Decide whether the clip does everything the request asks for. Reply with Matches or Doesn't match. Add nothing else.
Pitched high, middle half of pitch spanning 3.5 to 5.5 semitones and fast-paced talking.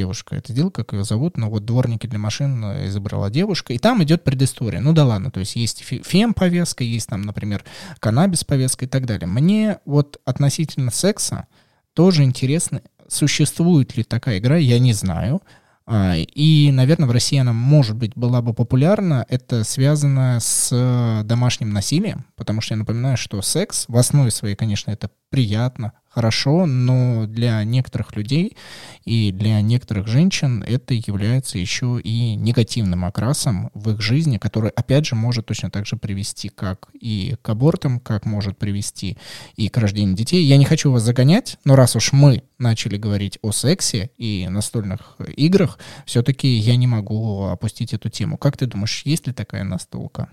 Doesn't match